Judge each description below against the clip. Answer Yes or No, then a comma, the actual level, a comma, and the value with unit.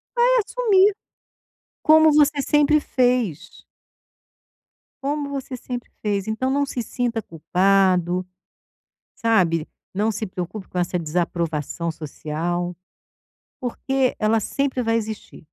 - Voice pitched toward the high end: Yes, high, 220 Hz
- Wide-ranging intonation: Yes, wide, 7.4 semitones